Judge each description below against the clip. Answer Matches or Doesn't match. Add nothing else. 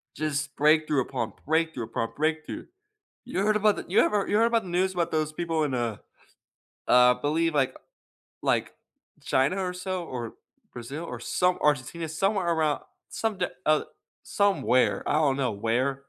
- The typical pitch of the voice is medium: Matches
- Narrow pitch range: Doesn't match